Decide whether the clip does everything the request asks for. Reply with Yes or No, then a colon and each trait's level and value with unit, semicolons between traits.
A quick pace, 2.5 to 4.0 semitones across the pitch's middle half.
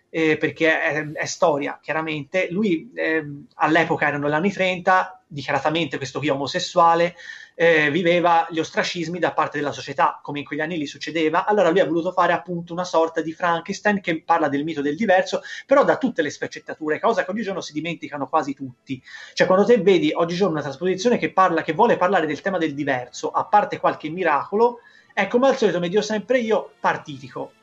Yes: fast, 190 wpm; average, 3.6 semitones